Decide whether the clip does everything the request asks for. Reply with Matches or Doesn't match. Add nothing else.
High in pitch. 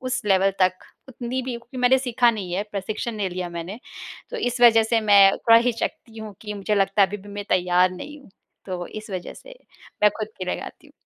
Matches